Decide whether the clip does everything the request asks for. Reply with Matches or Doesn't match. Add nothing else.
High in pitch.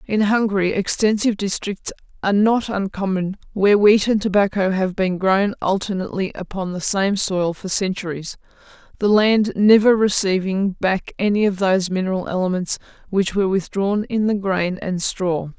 Matches